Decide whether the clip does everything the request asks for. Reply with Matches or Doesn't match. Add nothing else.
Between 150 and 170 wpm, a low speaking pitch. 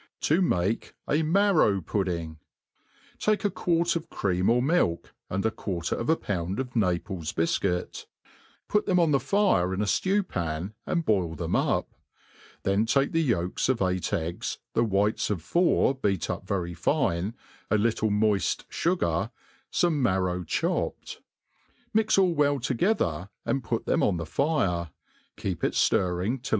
Matches